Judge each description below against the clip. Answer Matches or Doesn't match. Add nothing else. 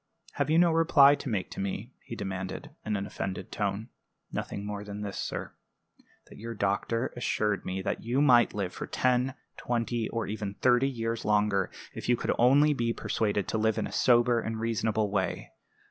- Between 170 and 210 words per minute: Matches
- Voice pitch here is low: Matches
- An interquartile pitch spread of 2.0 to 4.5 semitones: Matches